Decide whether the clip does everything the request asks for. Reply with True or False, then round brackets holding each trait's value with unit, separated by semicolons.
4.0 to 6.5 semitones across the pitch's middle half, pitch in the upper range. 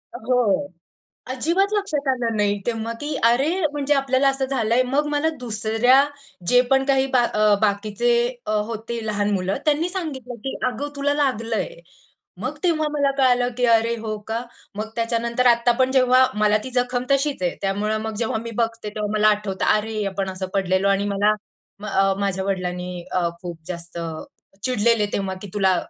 True (4.3 semitones; 230 Hz)